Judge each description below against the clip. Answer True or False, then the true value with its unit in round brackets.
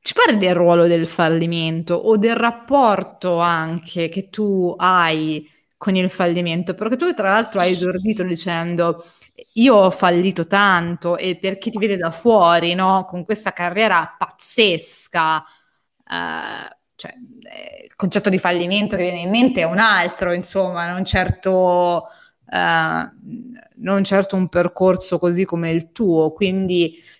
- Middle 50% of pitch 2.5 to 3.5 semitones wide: True (2.9 semitones)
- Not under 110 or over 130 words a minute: False (145 wpm)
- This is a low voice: False (185 Hz)